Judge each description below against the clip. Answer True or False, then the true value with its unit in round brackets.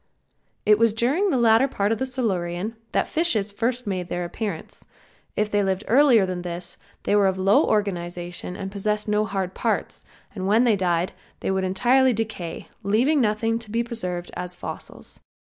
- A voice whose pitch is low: False (210 Hz)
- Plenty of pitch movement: False (3.8 semitones)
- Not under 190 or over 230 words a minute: False (175 wpm)